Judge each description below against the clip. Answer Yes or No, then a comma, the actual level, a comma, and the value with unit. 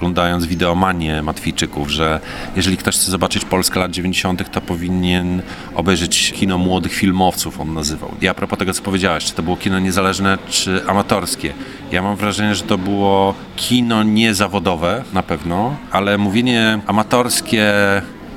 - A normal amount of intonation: No, narrow, 2.1 semitones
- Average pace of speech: Yes, average, 145 wpm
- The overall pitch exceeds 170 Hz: No, very low, 95 Hz